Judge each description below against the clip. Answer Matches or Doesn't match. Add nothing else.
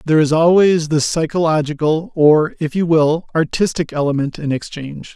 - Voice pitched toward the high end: Doesn't match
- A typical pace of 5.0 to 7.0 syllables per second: Matches